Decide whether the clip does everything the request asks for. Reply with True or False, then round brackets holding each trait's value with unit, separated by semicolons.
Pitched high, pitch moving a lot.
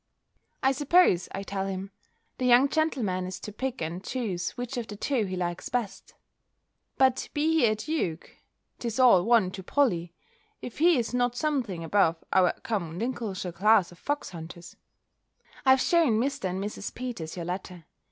True (210 Hz; 6.0 semitones)